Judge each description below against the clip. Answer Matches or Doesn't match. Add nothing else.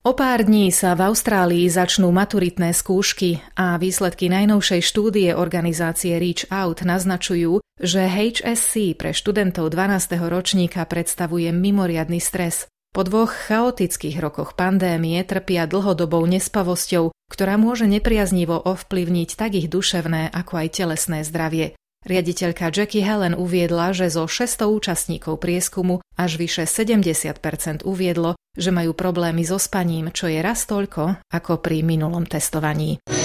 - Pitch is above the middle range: Doesn't match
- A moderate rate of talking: Matches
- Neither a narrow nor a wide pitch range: Doesn't match